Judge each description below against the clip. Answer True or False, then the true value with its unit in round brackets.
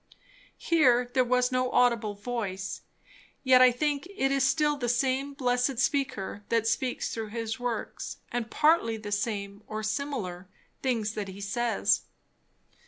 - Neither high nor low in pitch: False (245 Hz)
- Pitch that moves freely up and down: False (3.4 semitones)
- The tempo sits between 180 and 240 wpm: False (145 wpm)